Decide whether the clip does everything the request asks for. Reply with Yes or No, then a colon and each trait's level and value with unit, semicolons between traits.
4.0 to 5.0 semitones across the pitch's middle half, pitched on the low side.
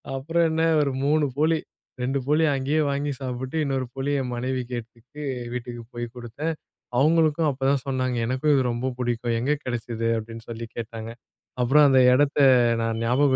No: average, 3.5 semitones; low, 130 Hz